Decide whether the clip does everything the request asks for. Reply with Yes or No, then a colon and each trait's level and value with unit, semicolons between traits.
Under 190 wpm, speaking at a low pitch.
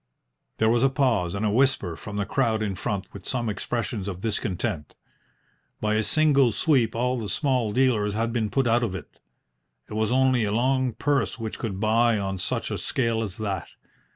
No: average, 195 wpm; low, 110 Hz